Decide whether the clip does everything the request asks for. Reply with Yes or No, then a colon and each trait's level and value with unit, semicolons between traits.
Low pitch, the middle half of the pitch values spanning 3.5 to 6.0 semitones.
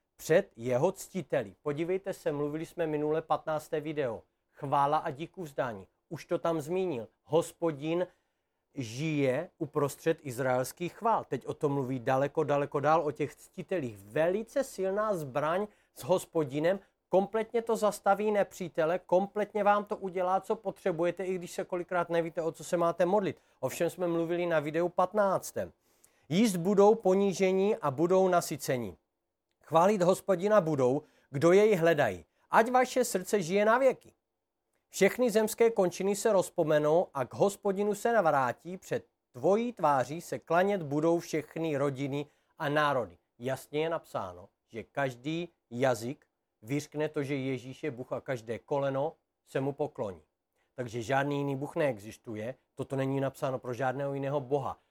No: medium, 165 Hz; average, 5.2 semitones